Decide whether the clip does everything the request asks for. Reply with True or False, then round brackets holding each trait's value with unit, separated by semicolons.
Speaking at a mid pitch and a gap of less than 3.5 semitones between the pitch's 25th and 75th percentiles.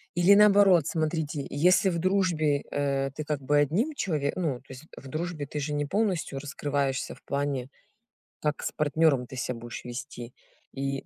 False (145 Hz; 3.9 semitones)